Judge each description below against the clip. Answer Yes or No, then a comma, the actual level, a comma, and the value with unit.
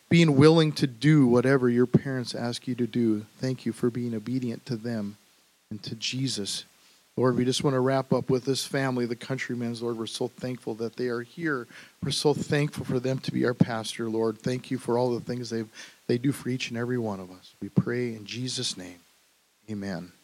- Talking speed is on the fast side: Yes, fast, 215 wpm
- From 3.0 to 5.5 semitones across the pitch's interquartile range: No, narrow, 2.4 semitones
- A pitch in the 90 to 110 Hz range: No, low, 125 Hz